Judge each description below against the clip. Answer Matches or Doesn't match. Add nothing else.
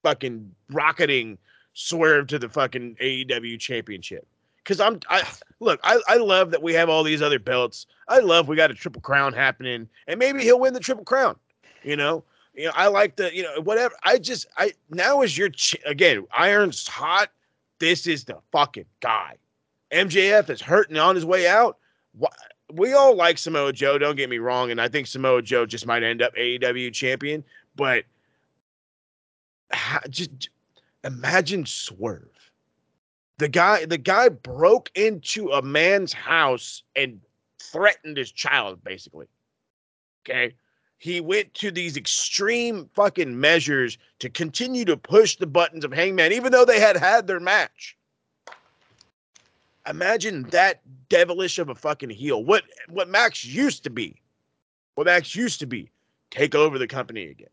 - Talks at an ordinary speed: Matches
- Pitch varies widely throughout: Matches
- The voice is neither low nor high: Matches